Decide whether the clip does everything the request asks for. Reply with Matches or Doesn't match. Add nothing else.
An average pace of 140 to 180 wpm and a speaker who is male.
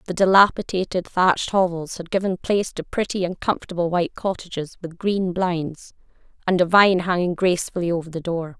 Doesn't match